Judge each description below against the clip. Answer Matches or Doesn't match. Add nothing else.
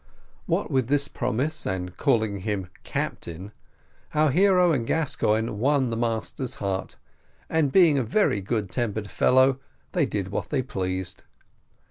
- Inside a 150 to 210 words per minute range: Doesn't match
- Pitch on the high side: Doesn't match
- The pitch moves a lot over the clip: Matches